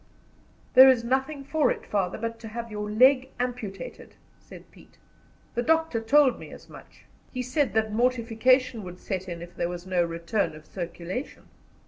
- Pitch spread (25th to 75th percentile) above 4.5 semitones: Yes, wide, 5.4 semitones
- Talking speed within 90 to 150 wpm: No, average, 170 wpm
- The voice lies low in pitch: No, high, 230 Hz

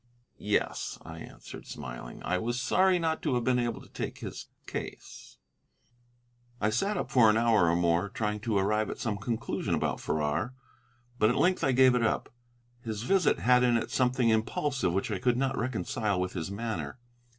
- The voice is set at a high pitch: No, low, 115 Hz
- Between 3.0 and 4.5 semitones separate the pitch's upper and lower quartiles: Yes, average, 3.9 semitones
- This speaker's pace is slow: No, average, 185 wpm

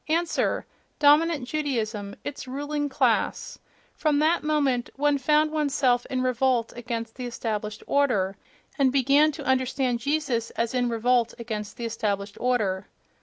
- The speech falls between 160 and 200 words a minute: No, average, 140 wpm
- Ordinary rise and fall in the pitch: Yes, average, 4.1 semitones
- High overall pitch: Yes, very high, 255 Hz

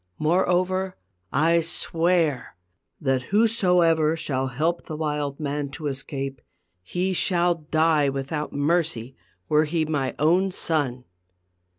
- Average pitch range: Yes, average, 3.6 semitones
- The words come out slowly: Yes, slow, 110 wpm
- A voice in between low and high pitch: Yes, medium, 155 Hz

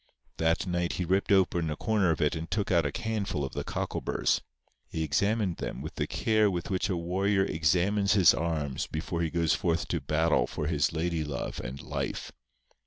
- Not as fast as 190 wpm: No, average, 195 wpm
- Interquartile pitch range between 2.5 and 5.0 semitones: Yes, average, 3.5 semitones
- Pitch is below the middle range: Yes, very low, 85 Hz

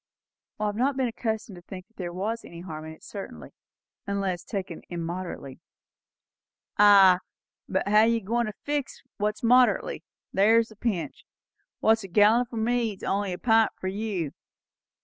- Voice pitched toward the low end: No, high, 205 Hz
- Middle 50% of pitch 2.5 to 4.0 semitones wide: Yes, average, 3.5 semitones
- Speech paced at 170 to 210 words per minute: No, average, 155 wpm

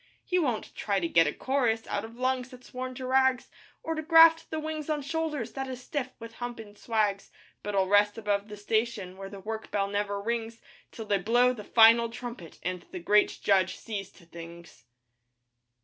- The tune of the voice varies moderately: Yes, average, 4.1 semitones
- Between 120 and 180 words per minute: No, average, 195 wpm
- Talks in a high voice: Yes, high, 225 Hz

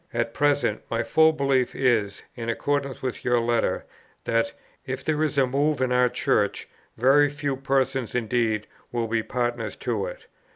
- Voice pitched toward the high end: No, low, 125 Hz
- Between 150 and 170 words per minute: Yes, average, 165 wpm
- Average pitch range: Yes, average, 3.1 semitones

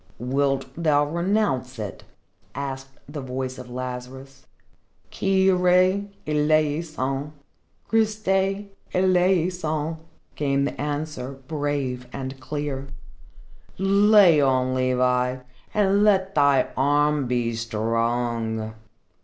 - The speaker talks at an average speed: No, slow, 85 wpm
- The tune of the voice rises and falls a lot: Yes, wide, 5.8 semitones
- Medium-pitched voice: Yes, medium, 145 Hz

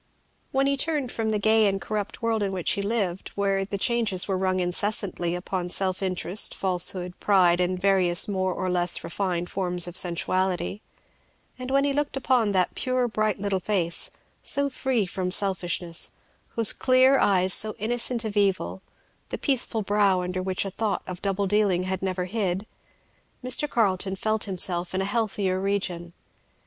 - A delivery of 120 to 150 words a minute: No, average, 170 wpm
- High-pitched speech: Yes, high, 195 Hz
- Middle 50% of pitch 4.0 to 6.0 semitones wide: No, average, 3.0 semitones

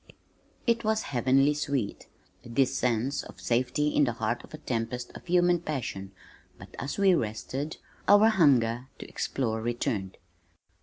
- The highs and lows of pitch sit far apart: No, average, 4.8 semitones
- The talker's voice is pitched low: Yes, low, 130 Hz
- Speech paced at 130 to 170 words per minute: Yes, average, 145 wpm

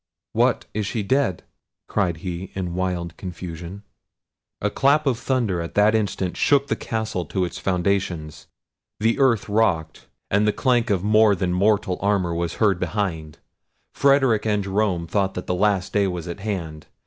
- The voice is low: Yes, low, 100 Hz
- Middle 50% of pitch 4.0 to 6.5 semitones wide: No, average, 3.5 semitones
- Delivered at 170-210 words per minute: No, average, 160 wpm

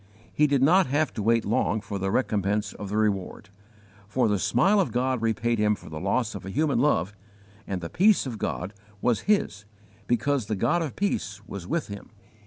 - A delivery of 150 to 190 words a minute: No, average, 200 wpm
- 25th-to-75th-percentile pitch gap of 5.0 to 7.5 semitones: Yes, average, 5.3 semitones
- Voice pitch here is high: No, low, 110 Hz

